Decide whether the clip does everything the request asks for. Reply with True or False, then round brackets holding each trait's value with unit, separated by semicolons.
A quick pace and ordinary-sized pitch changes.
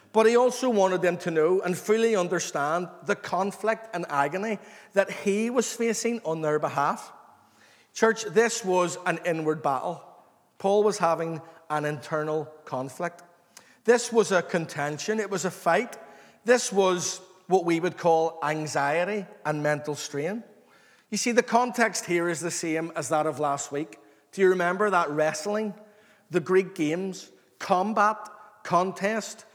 False (150 wpm; 4.6 semitones)